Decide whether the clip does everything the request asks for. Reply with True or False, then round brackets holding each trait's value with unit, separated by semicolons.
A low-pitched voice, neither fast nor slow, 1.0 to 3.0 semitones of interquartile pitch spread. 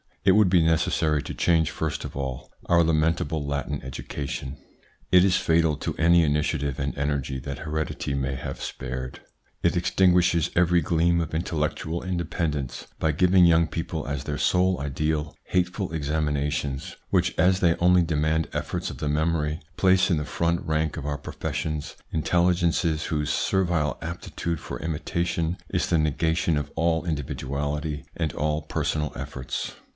True (80 Hz; 155 wpm; 2.6 semitones)